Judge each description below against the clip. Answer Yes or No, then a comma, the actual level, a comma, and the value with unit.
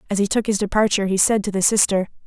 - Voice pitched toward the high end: Yes, high, 200 Hz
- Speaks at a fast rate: Yes, fast, 265 wpm